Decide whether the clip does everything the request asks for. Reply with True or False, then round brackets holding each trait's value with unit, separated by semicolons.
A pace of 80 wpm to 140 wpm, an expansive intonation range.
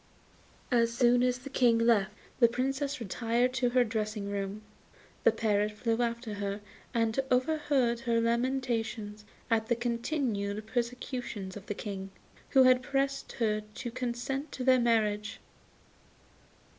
False (135 wpm; 2.8 semitones)